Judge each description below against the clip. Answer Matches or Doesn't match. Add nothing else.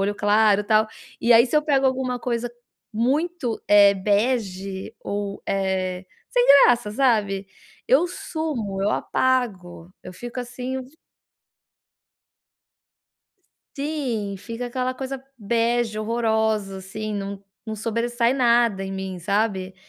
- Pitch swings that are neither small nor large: Matches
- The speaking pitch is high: Matches